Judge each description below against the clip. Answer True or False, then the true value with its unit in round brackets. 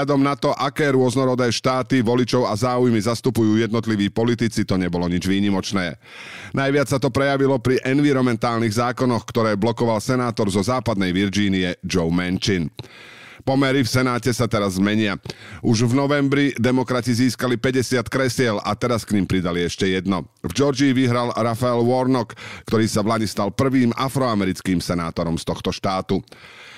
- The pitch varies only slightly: False (4.1 semitones)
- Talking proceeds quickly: False (150 wpm)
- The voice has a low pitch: True (120 Hz)